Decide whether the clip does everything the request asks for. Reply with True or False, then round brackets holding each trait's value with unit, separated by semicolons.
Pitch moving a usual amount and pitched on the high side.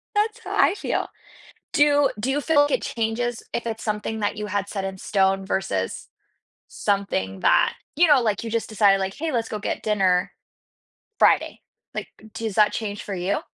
True (3.7 semitones; 210 Hz)